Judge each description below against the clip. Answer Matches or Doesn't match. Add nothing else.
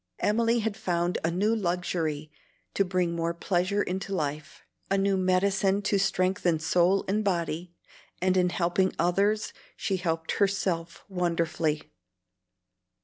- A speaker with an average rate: Doesn't match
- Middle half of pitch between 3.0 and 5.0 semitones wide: Doesn't match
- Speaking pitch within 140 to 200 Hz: Matches